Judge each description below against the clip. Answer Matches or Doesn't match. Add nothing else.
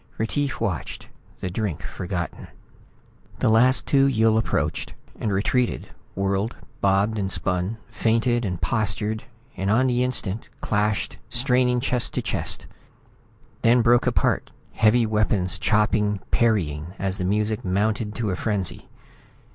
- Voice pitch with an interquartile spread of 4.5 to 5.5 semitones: Doesn't match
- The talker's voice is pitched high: Doesn't match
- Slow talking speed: Matches